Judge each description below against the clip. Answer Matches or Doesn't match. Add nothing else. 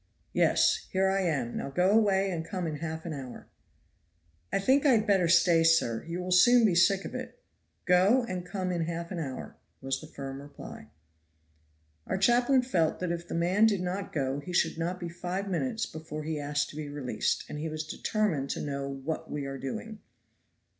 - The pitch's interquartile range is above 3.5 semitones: Matches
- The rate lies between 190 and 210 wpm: Matches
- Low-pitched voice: Doesn't match